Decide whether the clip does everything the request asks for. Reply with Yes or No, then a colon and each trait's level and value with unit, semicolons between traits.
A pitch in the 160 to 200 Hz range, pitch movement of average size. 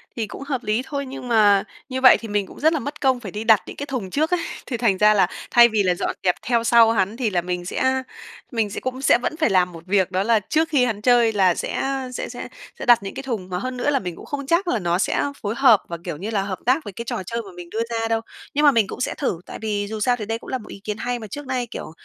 No: high, 225 Hz; average, 4.5 semitones